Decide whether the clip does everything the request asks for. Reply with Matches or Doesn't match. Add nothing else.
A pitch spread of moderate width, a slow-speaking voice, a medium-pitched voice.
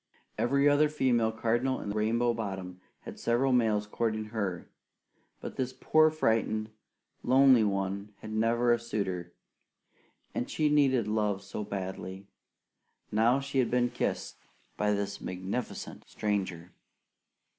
Doesn't match